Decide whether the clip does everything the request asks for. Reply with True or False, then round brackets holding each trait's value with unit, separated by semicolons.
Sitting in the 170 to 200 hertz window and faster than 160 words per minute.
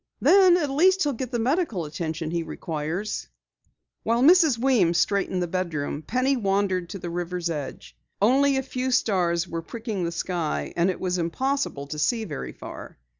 True (190 Hz; 175 wpm)